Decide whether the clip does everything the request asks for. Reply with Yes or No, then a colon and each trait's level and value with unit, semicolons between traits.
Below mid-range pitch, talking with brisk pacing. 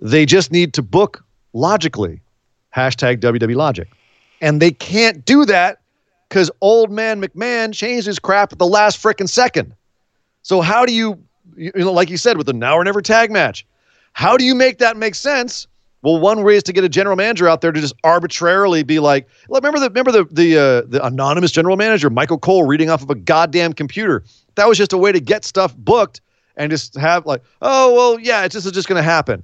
No: medium, 175 Hz; fast, 220 wpm